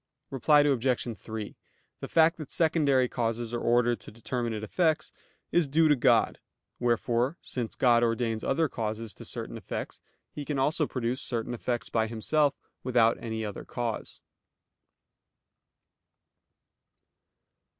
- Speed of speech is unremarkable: No, slow, 130 wpm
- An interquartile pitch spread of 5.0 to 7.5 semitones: No, average, 3.9 semitones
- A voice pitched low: Yes, low, 120 Hz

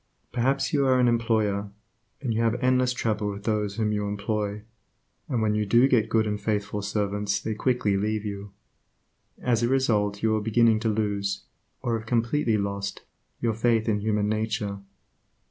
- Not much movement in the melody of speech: Yes, narrow, 2.2 semitones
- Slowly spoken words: No, average, 175 wpm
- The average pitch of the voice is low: Yes, low, 110 Hz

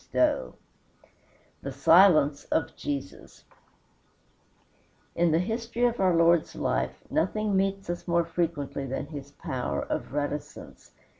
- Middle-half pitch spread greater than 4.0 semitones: Yes, average, 4.9 semitones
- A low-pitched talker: No, medium, 165 Hz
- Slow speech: Yes, slow, 120 wpm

